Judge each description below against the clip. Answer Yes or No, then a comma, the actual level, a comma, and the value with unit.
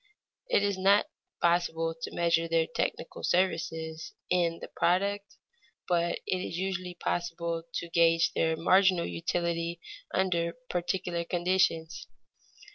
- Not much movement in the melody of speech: Yes, narrow, 1.8 semitones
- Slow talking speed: Yes, slow, 120 wpm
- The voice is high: No, medium, 170 Hz